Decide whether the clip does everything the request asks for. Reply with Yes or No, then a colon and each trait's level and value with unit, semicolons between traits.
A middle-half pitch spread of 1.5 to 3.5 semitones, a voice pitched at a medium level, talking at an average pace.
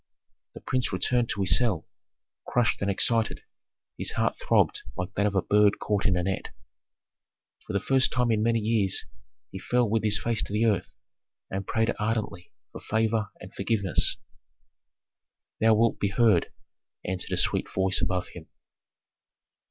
No: average, 2.9 semitones; low, 105 Hz; average, 160 wpm